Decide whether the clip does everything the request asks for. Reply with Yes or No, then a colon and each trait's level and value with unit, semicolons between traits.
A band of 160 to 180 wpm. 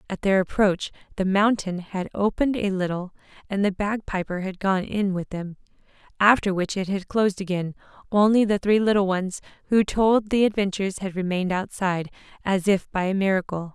Yes: average, 175 wpm